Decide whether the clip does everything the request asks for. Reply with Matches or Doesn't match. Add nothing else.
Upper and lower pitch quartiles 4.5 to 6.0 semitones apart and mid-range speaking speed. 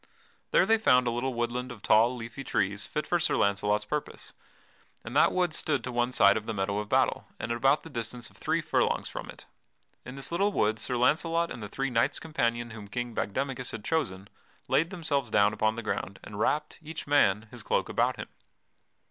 Doesn't match